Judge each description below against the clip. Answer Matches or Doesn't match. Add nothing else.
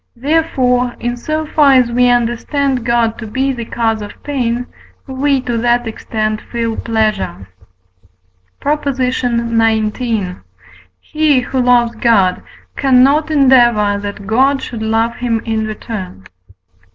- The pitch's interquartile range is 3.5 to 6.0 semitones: Doesn't match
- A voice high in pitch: Matches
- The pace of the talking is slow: Matches